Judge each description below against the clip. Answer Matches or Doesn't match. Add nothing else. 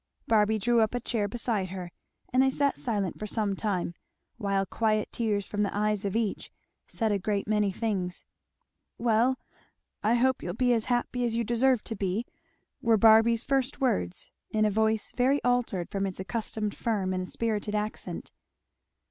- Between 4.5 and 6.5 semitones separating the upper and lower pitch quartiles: Doesn't match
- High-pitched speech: Matches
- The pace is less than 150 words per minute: Doesn't match